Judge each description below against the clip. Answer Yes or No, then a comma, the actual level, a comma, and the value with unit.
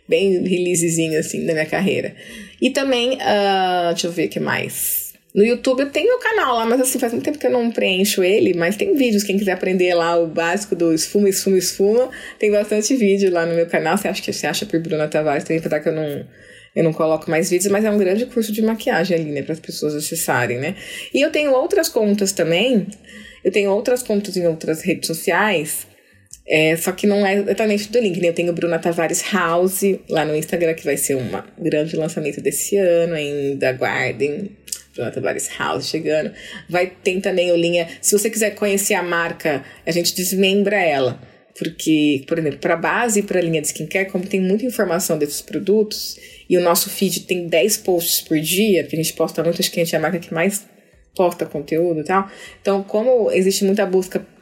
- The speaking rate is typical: No, fast, 215 wpm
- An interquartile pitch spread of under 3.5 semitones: No, average, 3.9 semitones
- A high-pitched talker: No, medium, 180 Hz